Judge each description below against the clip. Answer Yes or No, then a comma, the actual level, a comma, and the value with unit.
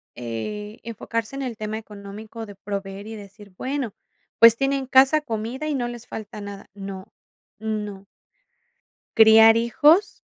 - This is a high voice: Yes, high, 220 Hz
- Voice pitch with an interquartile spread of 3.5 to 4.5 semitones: No, average, 2.9 semitones